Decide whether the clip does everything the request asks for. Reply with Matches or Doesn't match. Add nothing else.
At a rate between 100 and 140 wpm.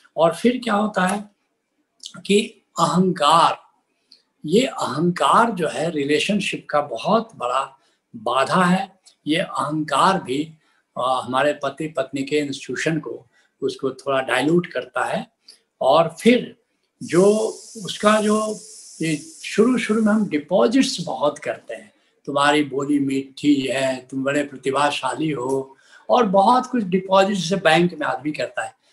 Matches